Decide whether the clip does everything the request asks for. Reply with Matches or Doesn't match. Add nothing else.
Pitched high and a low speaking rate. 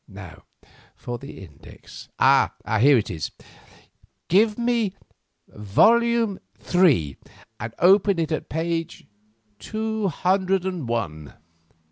Doesn't match